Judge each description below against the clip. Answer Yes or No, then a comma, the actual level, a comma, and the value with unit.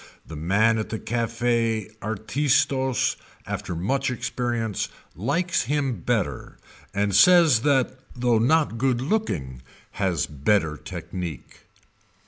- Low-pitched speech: Yes, low, 115 Hz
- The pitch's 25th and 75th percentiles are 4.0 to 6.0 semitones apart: Yes, wide, 5.5 semitones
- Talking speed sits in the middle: No, slow, 110 wpm